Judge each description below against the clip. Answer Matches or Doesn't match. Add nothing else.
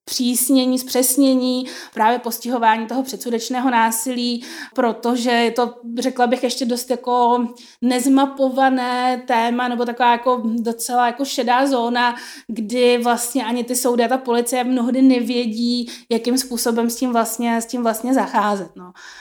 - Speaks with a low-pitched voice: Doesn't match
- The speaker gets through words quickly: Doesn't match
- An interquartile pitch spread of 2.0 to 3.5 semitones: Doesn't match